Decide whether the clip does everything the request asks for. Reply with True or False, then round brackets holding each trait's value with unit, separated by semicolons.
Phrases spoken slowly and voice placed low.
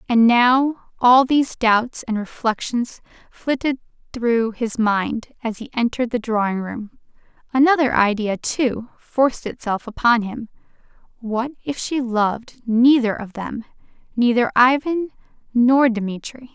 False (125 wpm; 240 Hz)